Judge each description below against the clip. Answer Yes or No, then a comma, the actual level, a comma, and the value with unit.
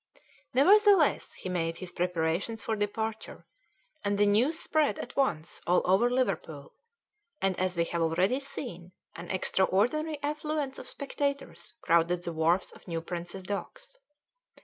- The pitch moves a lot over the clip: Yes, wide, 8.1 semitones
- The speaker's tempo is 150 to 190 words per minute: No, average, 140 wpm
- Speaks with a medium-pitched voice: No, high, 195 Hz